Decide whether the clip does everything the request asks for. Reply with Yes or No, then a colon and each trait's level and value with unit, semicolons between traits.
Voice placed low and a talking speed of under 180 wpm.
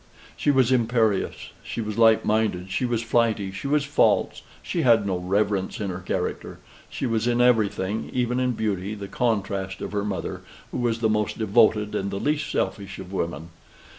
No: low, 110 Hz; average, 185 wpm